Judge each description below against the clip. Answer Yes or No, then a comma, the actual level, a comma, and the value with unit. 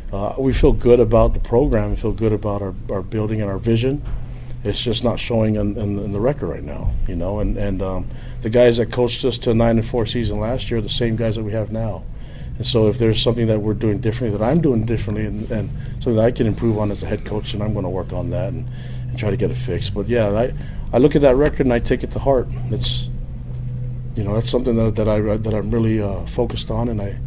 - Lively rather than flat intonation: No, average, 2.7 semitones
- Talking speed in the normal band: No, fast, 270 wpm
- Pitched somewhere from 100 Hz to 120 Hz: Yes, low, 115 Hz